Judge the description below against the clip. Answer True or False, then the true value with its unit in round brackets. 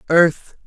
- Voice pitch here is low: False (165 Hz)